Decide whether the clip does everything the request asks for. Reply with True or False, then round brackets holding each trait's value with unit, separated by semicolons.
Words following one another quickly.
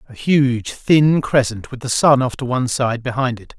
True (220 wpm)